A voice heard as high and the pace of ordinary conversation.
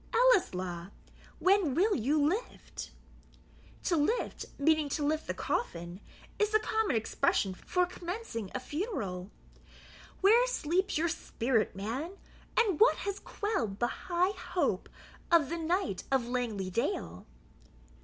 No: very high, 315 Hz; slow, 125 wpm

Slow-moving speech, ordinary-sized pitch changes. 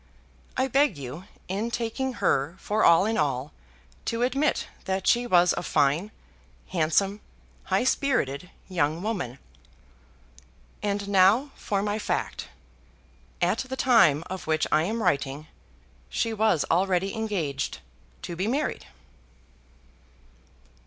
No: slow, 120 wpm; wide, 6.2 semitones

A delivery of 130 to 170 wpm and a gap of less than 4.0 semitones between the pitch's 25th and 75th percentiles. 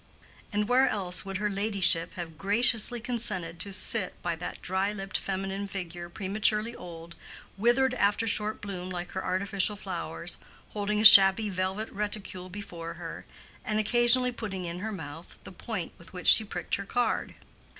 Yes: average, 160 wpm; average, 3.0 semitones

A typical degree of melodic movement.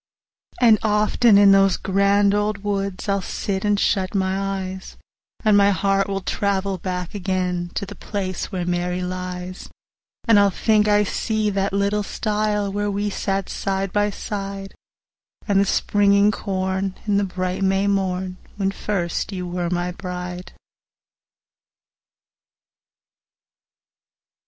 No: narrow, 1.7 semitones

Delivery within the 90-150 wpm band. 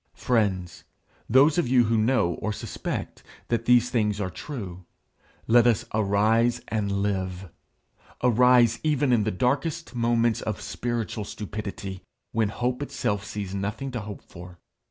Yes: average, 140 wpm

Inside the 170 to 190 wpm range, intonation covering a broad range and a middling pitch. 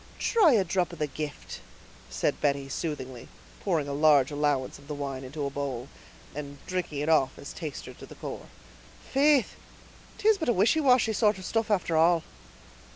Yes: average, 180 wpm; wide, 6.6 semitones; medium, 155 Hz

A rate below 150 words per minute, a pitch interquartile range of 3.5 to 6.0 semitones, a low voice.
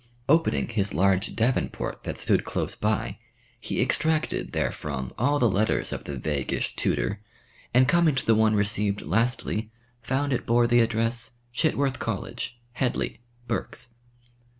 Yes: average, 140 wpm; average, 3.8 semitones; low, 115 Hz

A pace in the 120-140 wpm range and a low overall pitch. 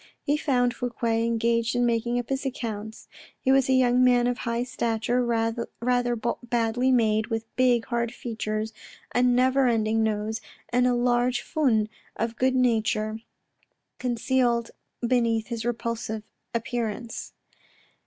No: slow, 135 wpm; high, 235 Hz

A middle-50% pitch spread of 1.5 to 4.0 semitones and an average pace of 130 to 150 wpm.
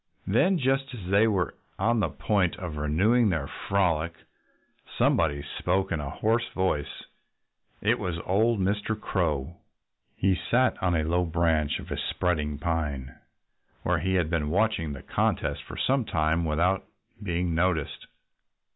No: average, 4.5 semitones; average, 145 wpm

